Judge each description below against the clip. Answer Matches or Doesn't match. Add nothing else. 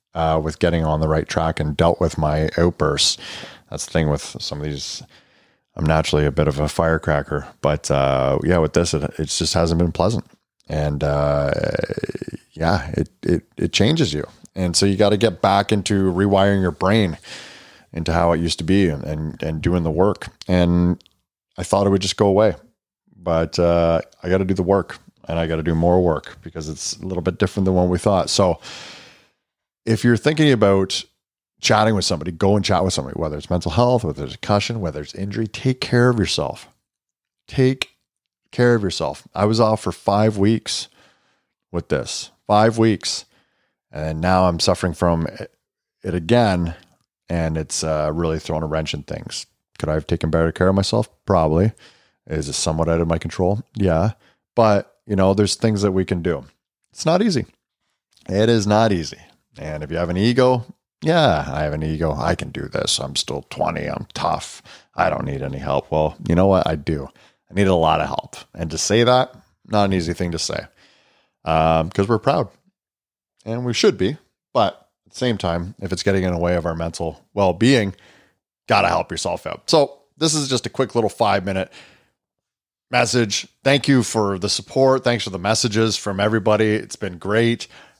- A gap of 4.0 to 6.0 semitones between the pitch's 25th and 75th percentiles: Matches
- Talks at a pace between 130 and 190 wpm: Doesn't match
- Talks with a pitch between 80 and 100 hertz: Matches